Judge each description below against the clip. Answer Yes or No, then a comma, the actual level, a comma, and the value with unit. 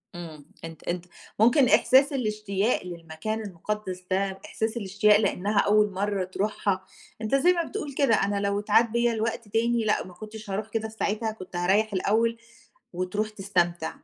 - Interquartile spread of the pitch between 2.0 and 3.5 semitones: Yes, average, 2.9 semitones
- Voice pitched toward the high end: Yes, high, 210 Hz